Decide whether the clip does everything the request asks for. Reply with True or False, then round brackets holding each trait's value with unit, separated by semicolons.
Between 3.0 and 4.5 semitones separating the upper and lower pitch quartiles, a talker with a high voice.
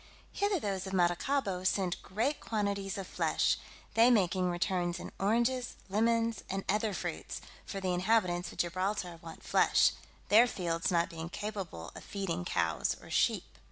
True (3.6 semitones; 195 Hz)